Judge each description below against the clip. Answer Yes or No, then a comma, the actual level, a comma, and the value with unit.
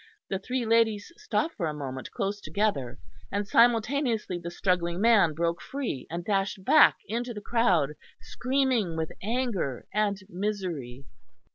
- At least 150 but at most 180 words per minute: No, average, 140 wpm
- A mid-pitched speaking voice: No, high, 205 Hz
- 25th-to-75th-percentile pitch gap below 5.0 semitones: No, average, 5.3 semitones